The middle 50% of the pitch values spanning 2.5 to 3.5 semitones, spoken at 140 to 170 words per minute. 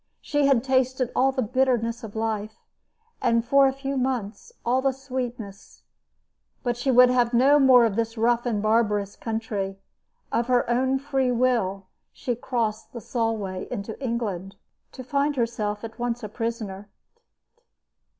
Yes: average, 2.9 semitones; average, 150 wpm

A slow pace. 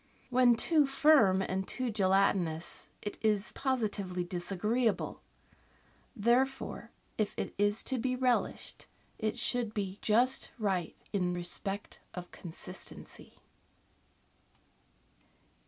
Yes: slow, 100 wpm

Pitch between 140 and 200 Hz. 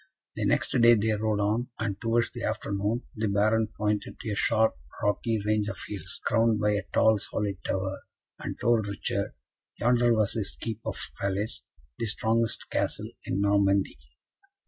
No: low, 105 Hz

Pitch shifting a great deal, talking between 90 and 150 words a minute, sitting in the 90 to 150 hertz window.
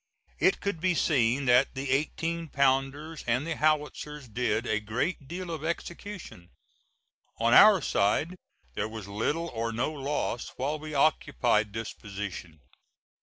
Yes: wide, 5.7 semitones; average, 140 wpm; low, 135 Hz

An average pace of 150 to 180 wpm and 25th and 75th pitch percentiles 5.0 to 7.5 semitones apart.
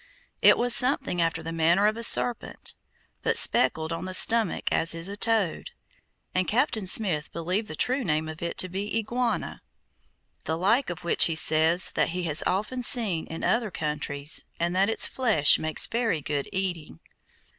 Yes: average, 175 wpm; wide, 5.5 semitones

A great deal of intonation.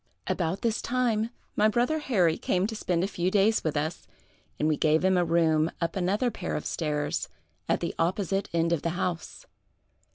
No: average, 4.3 semitones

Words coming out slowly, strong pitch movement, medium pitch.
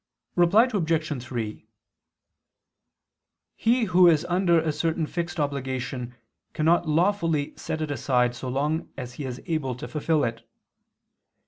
No: slow, 130 wpm; average, 4.6 semitones; medium, 155 Hz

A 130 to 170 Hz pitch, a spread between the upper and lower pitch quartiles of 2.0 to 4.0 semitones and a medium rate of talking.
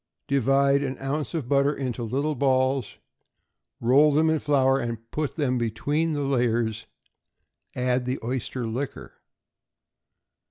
No: low, 135 Hz; narrow, 2.4 semitones; slow, 125 wpm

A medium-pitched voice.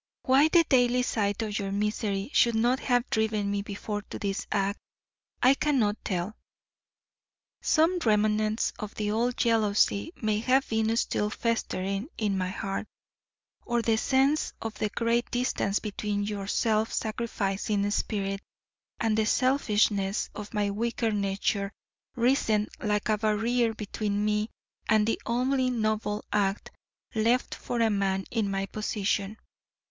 No: high, 215 Hz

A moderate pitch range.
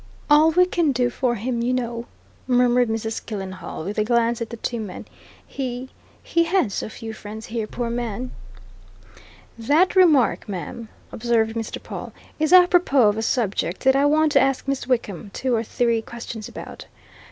Yes: average, 3.4 semitones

